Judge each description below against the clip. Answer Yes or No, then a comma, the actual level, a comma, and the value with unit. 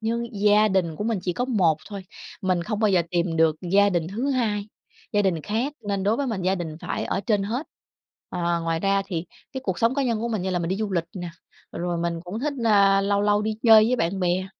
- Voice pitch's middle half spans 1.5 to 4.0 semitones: Yes, average, 3.7 semitones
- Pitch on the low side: No, high, 200 Hz